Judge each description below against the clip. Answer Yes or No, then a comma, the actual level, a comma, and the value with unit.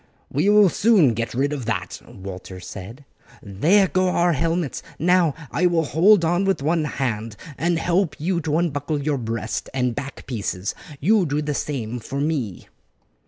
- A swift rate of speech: No, average, 165 wpm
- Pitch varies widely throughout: Yes, wide, 6.4 semitones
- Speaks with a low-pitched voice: No, medium, 150 Hz